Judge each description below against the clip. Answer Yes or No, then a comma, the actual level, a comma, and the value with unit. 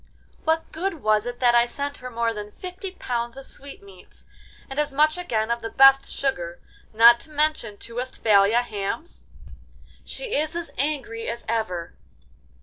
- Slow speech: No, average, 160 wpm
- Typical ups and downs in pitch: Yes, average, 4.9 semitones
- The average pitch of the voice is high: Yes, high, 245 Hz